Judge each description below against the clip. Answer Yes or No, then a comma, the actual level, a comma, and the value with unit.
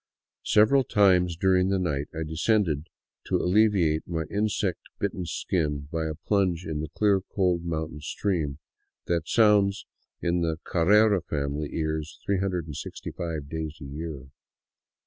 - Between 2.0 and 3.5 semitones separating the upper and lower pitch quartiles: No, average, 4.0 semitones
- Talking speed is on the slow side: Yes, slow, 130 wpm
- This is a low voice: Yes, very low, 85 Hz